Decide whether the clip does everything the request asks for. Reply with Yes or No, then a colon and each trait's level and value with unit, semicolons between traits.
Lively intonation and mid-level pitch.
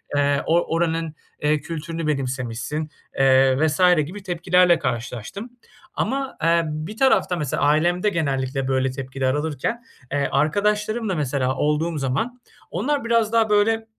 Yes: wide, 6.8 semitones; medium, 160 Hz